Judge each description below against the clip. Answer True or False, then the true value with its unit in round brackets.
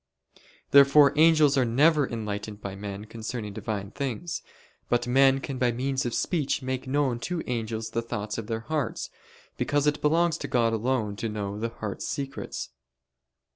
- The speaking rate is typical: True (165 wpm)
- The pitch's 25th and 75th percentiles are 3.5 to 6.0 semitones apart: True (4.3 semitones)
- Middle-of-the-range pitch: False (120 Hz)